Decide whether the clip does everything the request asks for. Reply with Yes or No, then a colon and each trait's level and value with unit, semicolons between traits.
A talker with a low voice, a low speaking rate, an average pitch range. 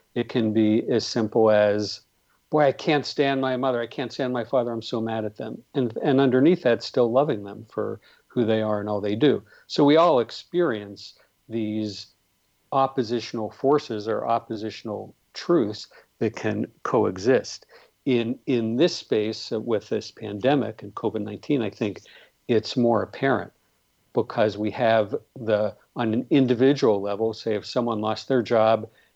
No: low, 115 Hz; average, 160 wpm; average, 3.1 semitones